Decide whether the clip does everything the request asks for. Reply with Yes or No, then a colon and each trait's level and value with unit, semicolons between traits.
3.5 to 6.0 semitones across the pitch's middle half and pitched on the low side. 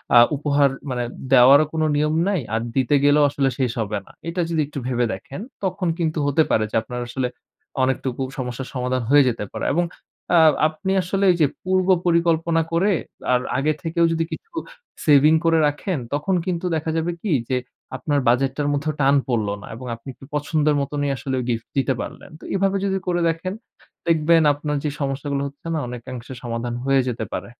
No: average, 4.1 semitones; medium, 145 Hz